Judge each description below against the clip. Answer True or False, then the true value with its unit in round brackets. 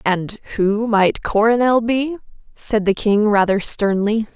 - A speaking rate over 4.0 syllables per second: False (3.8 syllables/s)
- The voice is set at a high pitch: True (215 Hz)